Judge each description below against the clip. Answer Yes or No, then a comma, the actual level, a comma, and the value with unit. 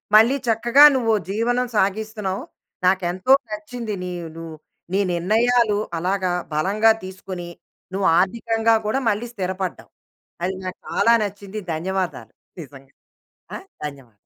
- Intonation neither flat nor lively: Yes, average, 3.4 semitones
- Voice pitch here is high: Yes, high, 200 Hz